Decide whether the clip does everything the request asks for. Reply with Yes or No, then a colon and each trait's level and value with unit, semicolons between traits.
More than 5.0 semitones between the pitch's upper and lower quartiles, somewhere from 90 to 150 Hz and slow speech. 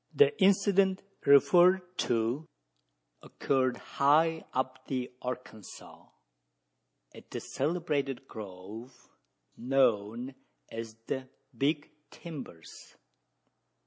Yes: wide, 5.4 semitones; low, 135 Hz; slow, 80 wpm